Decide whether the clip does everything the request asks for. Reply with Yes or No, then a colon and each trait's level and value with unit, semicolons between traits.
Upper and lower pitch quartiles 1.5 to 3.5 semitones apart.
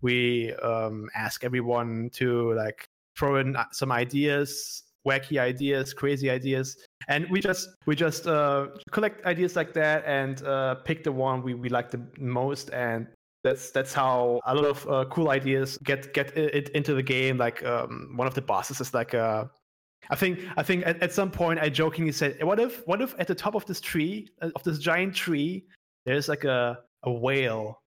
No: average, 4.2 semitones